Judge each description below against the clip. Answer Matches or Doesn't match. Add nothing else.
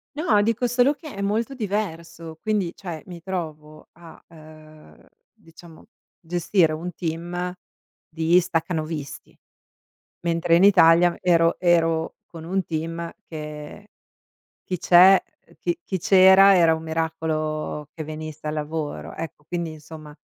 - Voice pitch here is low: Doesn't match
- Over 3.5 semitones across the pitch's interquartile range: Doesn't match